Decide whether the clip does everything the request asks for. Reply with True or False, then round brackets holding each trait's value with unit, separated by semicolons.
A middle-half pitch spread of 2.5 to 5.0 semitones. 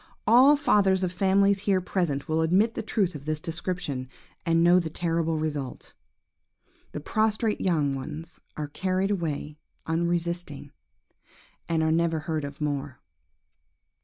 True (3.8 semitones)